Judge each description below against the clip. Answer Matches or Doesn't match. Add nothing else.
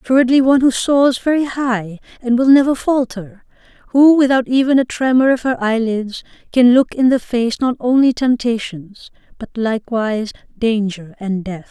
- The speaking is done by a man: Doesn't match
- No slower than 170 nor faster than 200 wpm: Doesn't match